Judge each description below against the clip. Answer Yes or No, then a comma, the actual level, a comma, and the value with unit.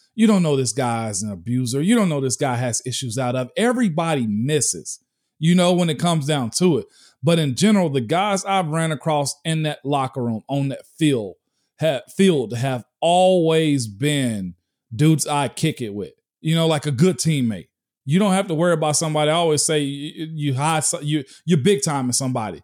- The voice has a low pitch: No, medium, 150 Hz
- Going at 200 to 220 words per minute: Yes, fast, 205 wpm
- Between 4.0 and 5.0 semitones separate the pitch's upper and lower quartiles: Yes, average, 4.6 semitones